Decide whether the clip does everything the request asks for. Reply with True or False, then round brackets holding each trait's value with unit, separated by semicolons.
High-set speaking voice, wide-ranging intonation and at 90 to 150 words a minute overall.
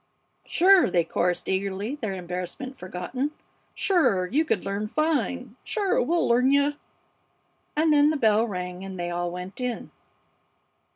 True (225 Hz; 8.3 semitones; 140 wpm)